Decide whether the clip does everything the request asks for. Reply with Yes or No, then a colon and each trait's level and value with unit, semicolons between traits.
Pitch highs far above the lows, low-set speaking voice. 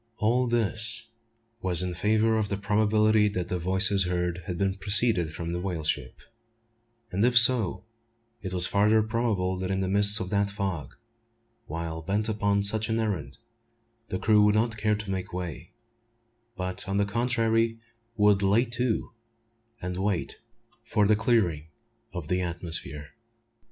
No: average, 3.2 semitones; low, 100 Hz